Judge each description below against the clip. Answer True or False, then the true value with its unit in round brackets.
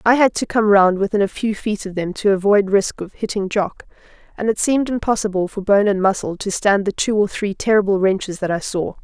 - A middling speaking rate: False (240 wpm)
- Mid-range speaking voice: False (200 Hz)